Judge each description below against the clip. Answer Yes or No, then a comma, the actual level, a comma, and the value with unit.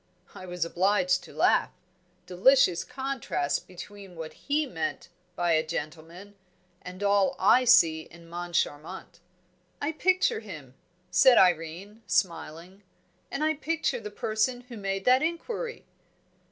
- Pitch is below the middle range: No, high, 190 Hz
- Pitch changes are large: Yes, wide, 6.7 semitones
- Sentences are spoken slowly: Yes, slow, 125 wpm